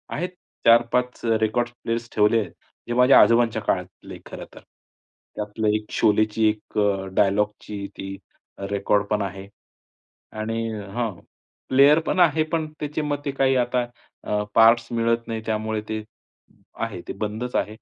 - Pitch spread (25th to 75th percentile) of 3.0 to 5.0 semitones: No, narrow, 2.5 semitones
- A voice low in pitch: Yes, low, 115 Hz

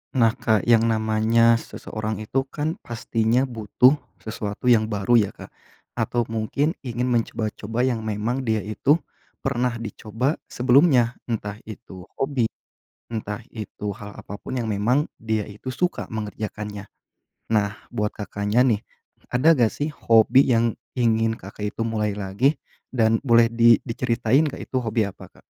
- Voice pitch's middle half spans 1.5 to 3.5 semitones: Yes, narrow, 2.6 semitones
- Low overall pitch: Yes, low, 115 Hz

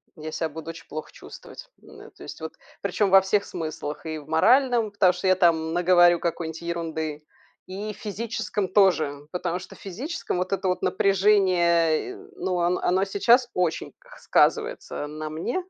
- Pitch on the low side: No, medium, 180 Hz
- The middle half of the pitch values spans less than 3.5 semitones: No, average, 3.9 semitones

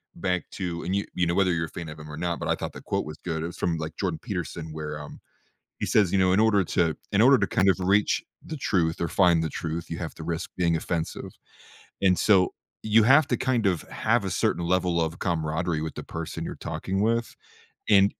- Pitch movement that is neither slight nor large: Yes, average, 3.3 semitones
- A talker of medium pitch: No, very low, 85 Hz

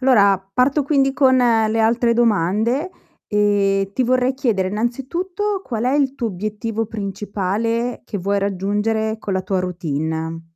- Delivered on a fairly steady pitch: No, average, 4.2 semitones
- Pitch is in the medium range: No, high, 220 Hz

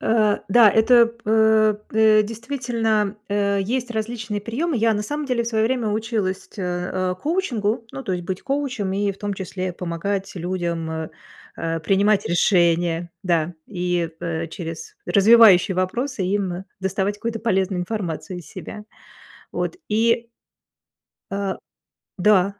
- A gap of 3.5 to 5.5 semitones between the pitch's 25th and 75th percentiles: Yes, average, 3.8 semitones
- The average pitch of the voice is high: Yes, high, 205 Hz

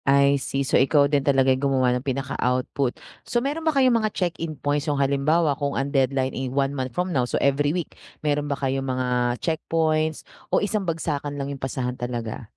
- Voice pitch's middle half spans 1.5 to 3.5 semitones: Yes, average, 2.8 semitones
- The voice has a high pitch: No, medium, 140 Hz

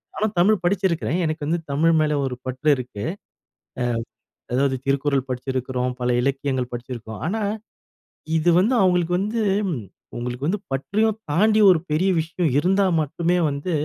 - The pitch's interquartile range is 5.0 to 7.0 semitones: Yes, wide, 5.6 semitones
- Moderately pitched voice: Yes, medium, 155 Hz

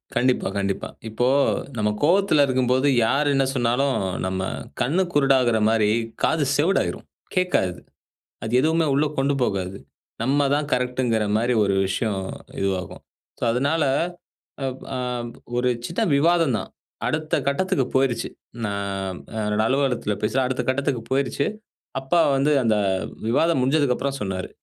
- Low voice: Yes, low, 130 Hz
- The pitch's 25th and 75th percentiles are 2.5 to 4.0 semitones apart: No, average, 4.6 semitones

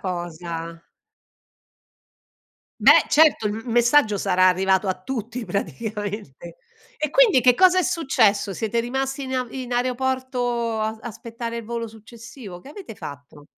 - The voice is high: Yes, high, 230 Hz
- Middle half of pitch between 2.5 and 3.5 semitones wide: No, average, 4.6 semitones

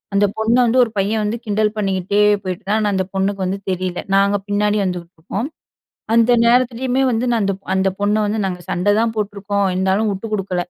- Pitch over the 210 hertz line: No, high, 205 Hz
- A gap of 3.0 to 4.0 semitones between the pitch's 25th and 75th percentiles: No, narrow, 2.4 semitones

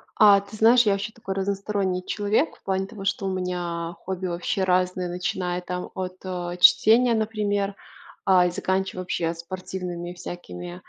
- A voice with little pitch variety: Yes, narrow, 2.1 semitones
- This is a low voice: No, medium, 185 Hz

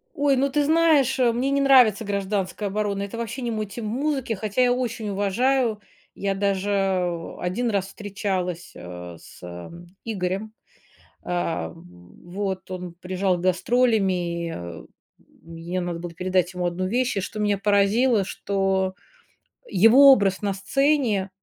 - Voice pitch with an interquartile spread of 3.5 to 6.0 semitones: Yes, average, 4.3 semitones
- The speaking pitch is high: Yes, high, 200 Hz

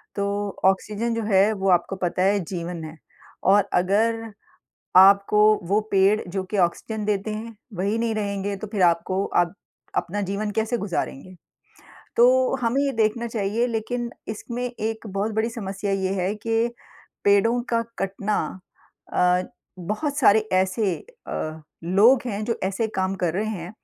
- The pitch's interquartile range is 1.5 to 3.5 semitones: Yes, average, 2.8 semitones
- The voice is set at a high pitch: Yes, high, 205 Hz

